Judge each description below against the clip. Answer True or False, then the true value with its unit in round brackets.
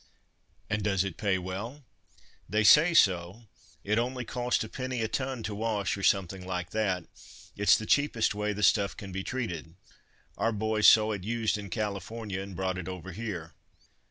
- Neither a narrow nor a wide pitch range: True (3.1 semitones)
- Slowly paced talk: False (180 wpm)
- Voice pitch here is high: False (105 Hz)